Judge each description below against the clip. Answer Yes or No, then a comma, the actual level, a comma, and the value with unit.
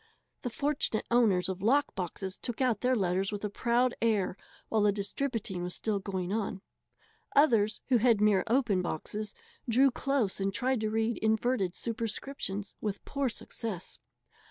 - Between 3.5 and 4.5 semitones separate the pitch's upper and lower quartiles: Yes, average, 3.8 semitones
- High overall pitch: Yes, high, 215 Hz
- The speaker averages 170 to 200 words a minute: No, average, 155 wpm